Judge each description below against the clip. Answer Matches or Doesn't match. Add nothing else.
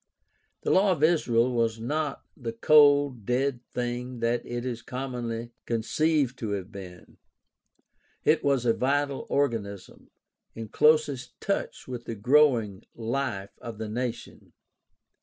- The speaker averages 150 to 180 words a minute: Doesn't match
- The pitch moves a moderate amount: Matches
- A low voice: Matches